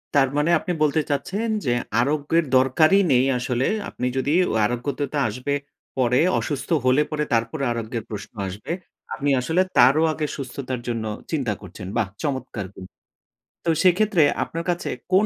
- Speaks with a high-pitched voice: No, low, 135 Hz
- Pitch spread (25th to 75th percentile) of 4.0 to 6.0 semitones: Yes, average, 4.3 semitones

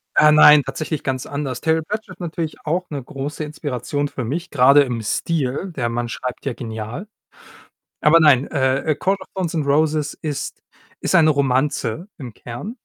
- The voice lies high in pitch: No, medium, 145 Hz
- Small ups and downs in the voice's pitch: No, average, 3.6 semitones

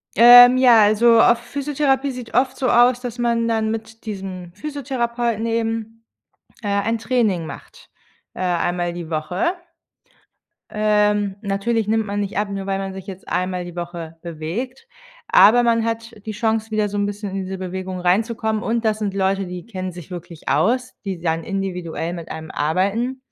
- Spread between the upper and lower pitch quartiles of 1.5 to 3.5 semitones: No, average, 4.0 semitones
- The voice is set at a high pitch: Yes, high, 210 Hz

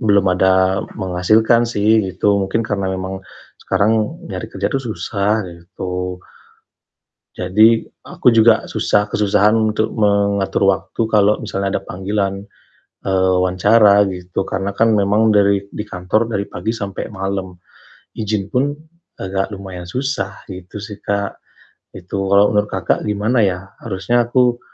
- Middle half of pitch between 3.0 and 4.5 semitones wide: No, narrow, 2.4 semitones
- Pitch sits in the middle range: No, low, 100 Hz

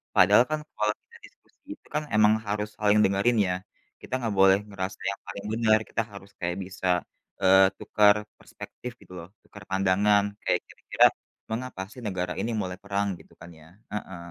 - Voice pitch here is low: Yes, low, 100 Hz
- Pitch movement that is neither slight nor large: No, narrow, 2.1 semitones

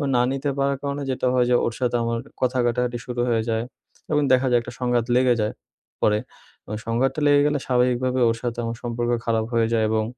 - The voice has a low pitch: Yes, low, 125 Hz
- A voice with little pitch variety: Yes, narrow, 1.8 semitones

